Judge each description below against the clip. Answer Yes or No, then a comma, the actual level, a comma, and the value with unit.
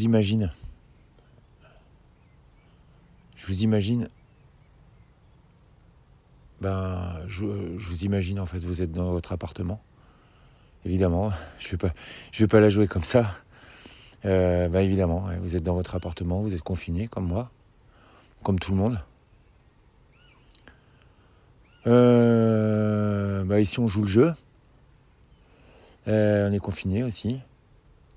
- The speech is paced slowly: Yes, slow, 120 wpm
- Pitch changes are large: No, average, 3.9 semitones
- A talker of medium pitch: No, low, 100 Hz